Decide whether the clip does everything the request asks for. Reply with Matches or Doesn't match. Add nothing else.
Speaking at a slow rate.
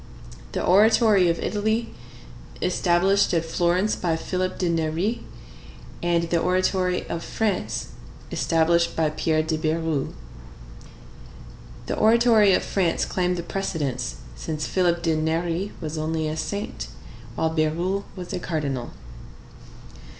Matches